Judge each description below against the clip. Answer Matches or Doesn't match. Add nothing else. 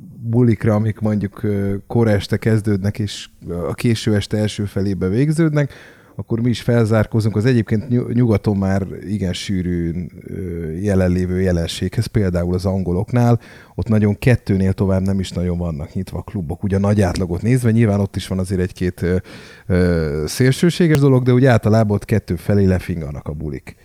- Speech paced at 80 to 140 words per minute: Doesn't match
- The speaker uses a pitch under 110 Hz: Matches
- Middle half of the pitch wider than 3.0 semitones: Matches